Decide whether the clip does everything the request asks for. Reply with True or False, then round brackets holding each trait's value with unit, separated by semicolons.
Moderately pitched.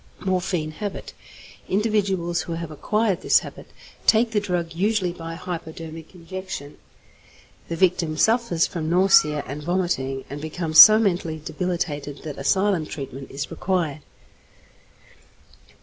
True (170 Hz)